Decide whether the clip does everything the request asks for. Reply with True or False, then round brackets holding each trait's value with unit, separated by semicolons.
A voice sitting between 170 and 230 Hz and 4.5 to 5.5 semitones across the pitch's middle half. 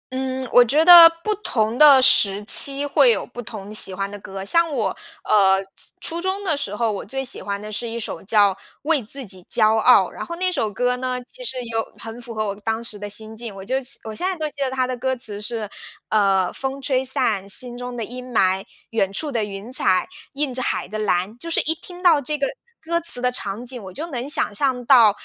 False (245 Hz; 4.9 semitones)